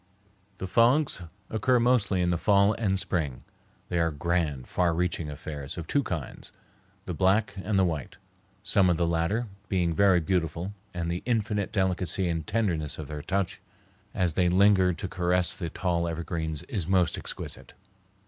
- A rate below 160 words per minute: No, average, 165 wpm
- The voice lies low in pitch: Yes, very low, 90 Hz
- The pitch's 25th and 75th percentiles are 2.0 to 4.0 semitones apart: Yes, average, 3.0 semitones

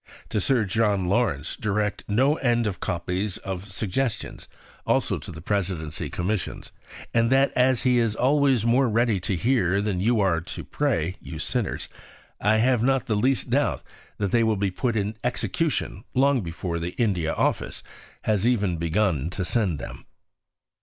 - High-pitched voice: No, low, 105 Hz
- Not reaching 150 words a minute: No, average, 165 wpm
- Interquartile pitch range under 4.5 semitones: No, average, 4.8 semitones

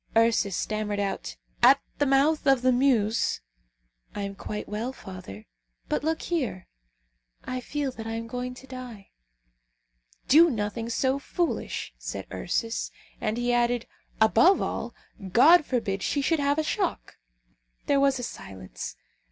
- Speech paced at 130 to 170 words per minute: Yes, average, 150 wpm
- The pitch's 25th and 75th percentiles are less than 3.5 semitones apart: No, average, 4.8 semitones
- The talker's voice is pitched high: Yes, high, 240 Hz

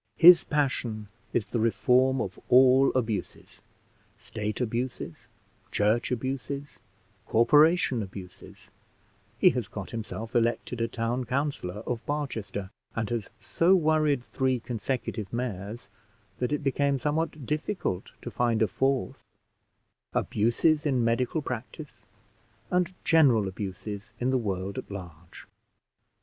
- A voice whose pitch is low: Yes, low, 120 Hz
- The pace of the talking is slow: Yes, slow, 120 wpm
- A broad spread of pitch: No, average, 4.3 semitones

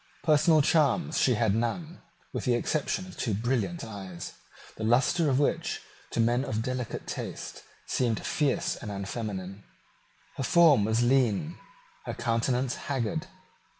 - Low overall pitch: Yes, low, 125 Hz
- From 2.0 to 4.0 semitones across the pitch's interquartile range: No, average, 5.1 semitones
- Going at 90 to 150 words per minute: Yes, average, 140 wpm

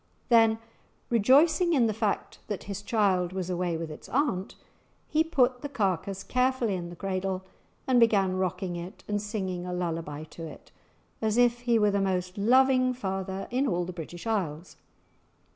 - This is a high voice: Yes, high, 200 Hz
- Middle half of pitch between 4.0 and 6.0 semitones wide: Yes, average, 4.8 semitones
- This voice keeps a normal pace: Yes, average, 170 wpm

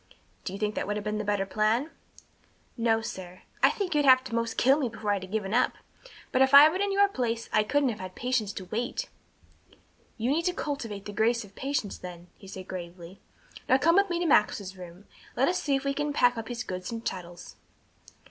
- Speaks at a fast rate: Yes, fast, 235 wpm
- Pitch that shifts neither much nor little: No, wide, 5.7 semitones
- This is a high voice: Yes, high, 225 Hz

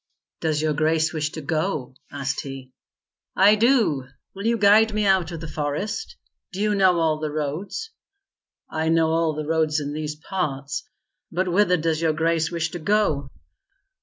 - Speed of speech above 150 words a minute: Yes, average, 170 wpm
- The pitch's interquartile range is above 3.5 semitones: Yes, average, 4.0 semitones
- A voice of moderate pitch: Yes, medium, 160 Hz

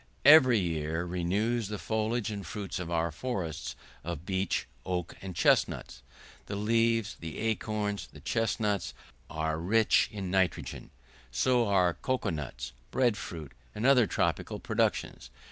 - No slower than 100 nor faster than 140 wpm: Yes, slow, 135 wpm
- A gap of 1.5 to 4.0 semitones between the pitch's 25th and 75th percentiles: No, average, 4.8 semitones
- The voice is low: Yes, low, 100 Hz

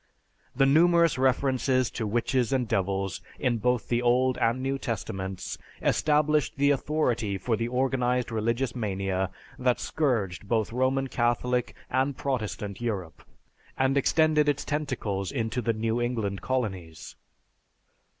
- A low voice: Yes, low, 125 Hz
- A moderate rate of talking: No, slow, 130 wpm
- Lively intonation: No, average, 3.7 semitones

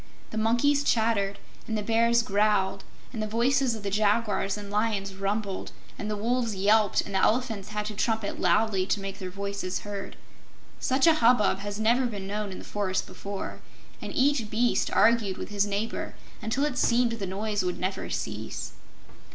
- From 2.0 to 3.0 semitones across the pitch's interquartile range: Yes, narrow, 2.5 semitones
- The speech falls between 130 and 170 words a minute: No, average, 180 wpm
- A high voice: Yes, high, 210 Hz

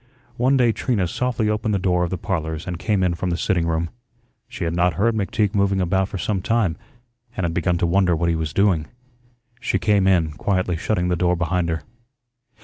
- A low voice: Yes, very low, 90 Hz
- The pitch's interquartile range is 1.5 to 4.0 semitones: Yes, average, 2.9 semitones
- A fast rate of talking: Yes, fast, 215 wpm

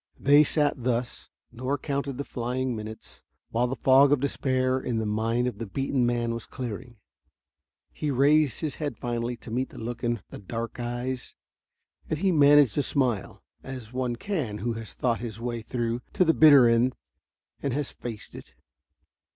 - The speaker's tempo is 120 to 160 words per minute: No, average, 175 wpm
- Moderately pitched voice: No, low, 125 Hz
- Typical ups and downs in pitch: Yes, average, 3.0 semitones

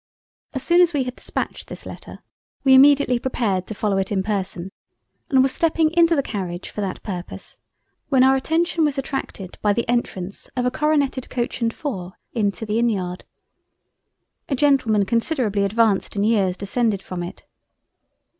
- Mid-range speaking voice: No, high, 230 Hz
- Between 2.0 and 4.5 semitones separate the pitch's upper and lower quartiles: No, wide, 5.4 semitones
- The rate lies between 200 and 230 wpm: No, average, 170 wpm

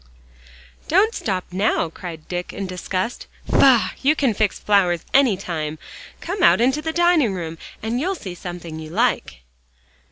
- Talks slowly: No, average, 155 wpm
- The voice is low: No, high, 200 Hz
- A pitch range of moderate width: No, wide, 7.5 semitones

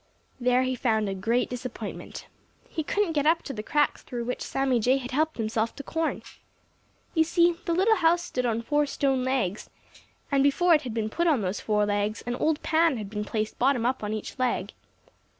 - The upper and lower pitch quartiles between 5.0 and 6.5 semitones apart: Yes, wide, 5.6 semitones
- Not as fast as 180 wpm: No, fast, 205 wpm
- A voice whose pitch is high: Yes, very high, 255 Hz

